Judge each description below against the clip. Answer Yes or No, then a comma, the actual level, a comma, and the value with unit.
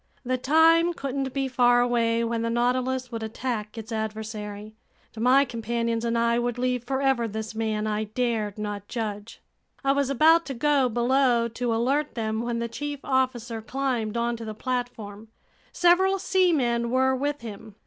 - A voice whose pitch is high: Yes, high, 240 Hz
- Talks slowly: No, average, 165 wpm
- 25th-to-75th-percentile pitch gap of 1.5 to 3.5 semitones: Yes, average, 2.8 semitones